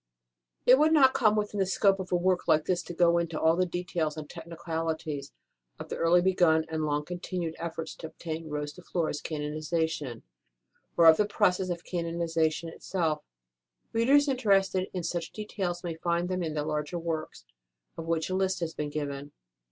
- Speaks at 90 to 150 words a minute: No, average, 185 wpm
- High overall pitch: No, medium, 170 Hz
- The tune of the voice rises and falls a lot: No, narrow, 2.6 semitones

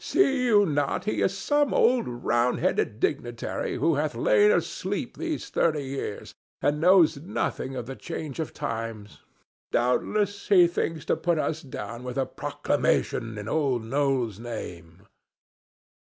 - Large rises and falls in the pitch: Yes, wide, 7.3 semitones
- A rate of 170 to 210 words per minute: No, average, 145 wpm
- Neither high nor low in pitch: Yes, medium, 145 Hz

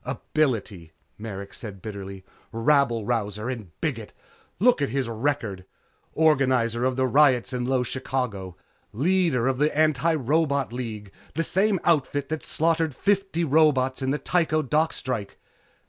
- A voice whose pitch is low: Yes, low, 130 Hz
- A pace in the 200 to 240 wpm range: No, average, 140 wpm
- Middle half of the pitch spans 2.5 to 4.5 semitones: No, average, 5.1 semitones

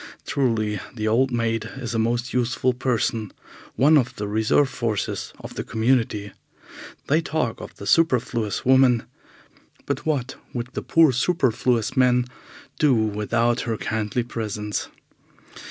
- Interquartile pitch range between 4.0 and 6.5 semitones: No, average, 2.7 semitones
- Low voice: Yes, low, 120 Hz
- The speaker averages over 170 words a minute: No, slow, 135 wpm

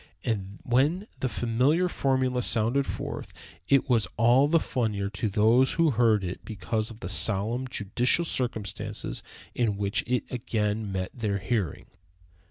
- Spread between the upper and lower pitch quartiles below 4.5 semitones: Yes, average, 3.7 semitones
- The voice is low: Yes, low, 115 Hz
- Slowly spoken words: No, average, 145 wpm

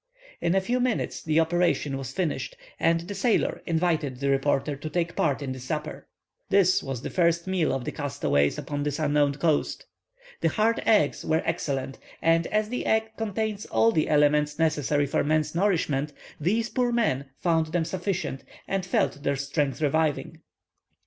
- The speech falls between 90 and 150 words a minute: No, average, 170 wpm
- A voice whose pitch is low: No, medium, 160 Hz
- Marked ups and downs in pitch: No, average, 4.5 semitones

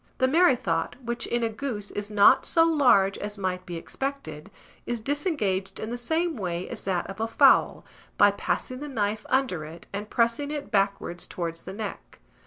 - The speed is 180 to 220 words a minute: Yes, average, 185 wpm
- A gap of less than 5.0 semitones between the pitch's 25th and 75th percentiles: No, wide, 5.5 semitones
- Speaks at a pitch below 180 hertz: No, high, 215 Hz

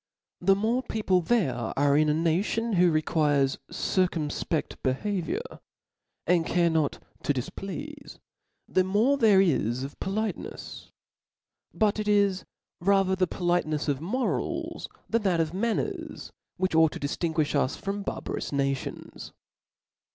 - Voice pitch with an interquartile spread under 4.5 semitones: No, average, 5.0 semitones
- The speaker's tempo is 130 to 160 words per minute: Yes, average, 145 wpm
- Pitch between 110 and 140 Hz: No, medium, 180 Hz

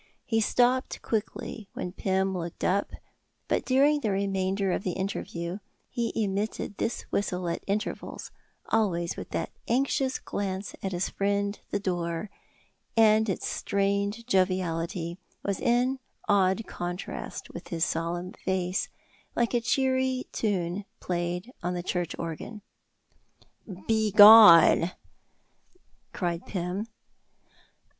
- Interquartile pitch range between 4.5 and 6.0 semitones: No, average, 3.7 semitones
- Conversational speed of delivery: No, slow, 115 wpm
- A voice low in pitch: No, high, 195 Hz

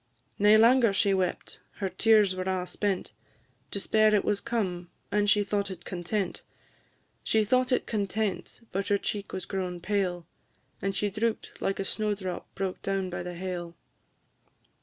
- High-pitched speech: Yes, high, 195 Hz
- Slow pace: No, average, 160 wpm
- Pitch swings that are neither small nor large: No, narrow, 2.2 semitones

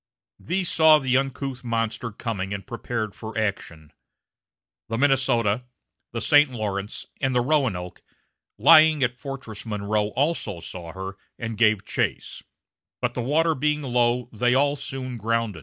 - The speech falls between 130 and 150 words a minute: Yes, average, 140 wpm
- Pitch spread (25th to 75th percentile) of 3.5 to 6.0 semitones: Yes, average, 4.3 semitones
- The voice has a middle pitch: No, low, 120 Hz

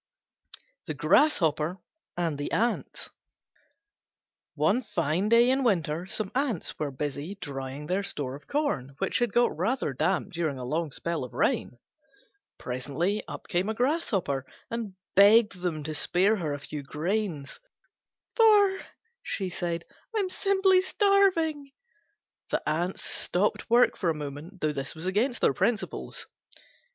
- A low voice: No, medium, 180 Hz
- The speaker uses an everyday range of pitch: No, wide, 7.9 semitones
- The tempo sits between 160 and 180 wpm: No, average, 140 wpm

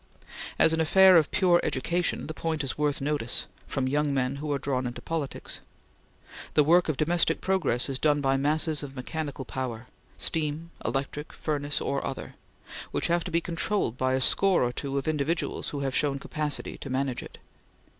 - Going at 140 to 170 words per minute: No, average, 185 wpm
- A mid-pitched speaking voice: Yes, medium, 145 Hz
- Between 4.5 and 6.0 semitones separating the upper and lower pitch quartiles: No, average, 3.2 semitones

